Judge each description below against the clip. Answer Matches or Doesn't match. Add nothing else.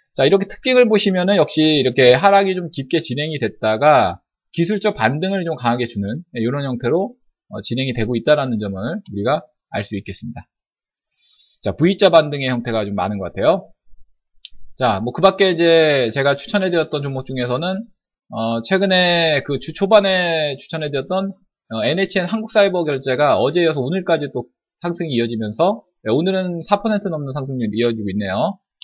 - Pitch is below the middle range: Doesn't match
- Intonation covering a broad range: Matches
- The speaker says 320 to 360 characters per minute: Matches